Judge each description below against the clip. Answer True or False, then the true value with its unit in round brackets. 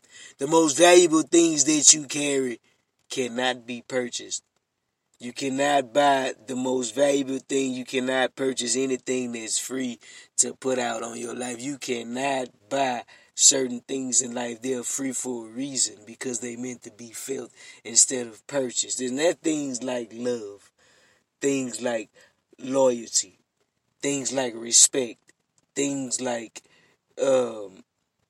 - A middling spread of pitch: False (2.2 semitones)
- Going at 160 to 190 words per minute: False (140 wpm)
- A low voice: True (130 Hz)